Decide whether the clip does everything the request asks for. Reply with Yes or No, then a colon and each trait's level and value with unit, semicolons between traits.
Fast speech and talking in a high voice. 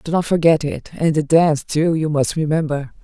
No: fast, 215 wpm; medium, 155 Hz